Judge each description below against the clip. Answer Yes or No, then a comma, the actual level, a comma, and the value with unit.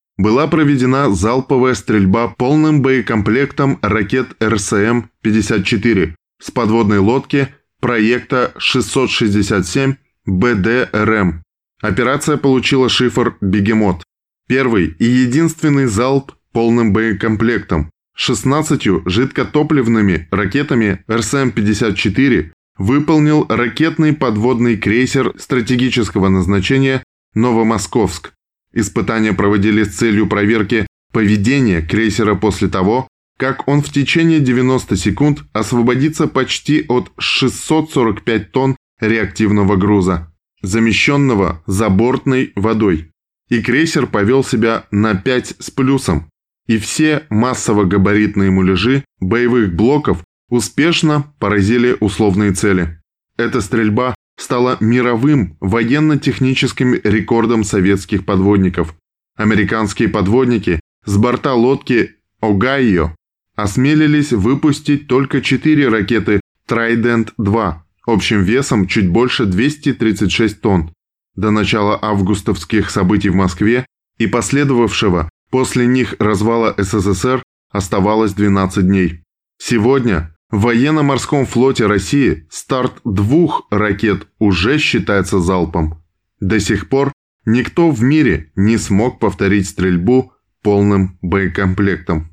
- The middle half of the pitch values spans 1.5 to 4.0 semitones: No, average, 4.5 semitones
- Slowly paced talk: Yes, slow, 95 wpm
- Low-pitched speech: Yes, low, 110 Hz